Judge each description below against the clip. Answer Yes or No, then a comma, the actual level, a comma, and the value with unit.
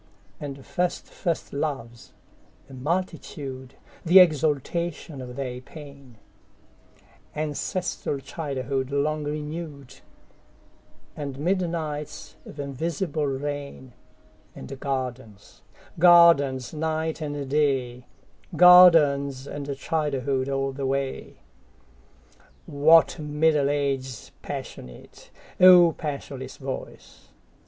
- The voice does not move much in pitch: No, average, 3.0 semitones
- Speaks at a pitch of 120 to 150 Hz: Yes, medium, 140 Hz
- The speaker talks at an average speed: No, slow, 70 wpm